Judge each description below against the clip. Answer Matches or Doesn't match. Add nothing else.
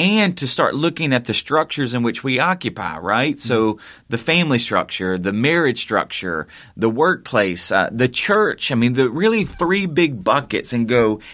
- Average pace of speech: Matches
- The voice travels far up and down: Matches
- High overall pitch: Doesn't match